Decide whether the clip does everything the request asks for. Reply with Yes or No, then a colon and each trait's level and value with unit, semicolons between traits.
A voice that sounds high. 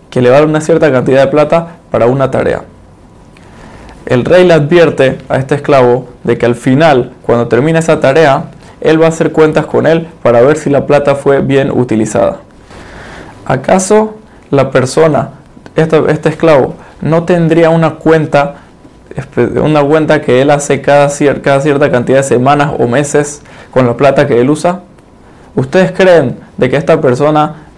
No: medium, 145 Hz